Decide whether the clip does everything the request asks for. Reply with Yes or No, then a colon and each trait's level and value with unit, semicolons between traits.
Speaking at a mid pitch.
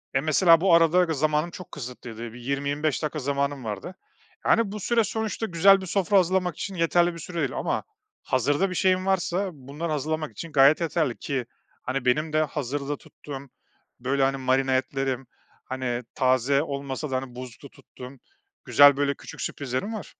Yes: medium, 145 Hz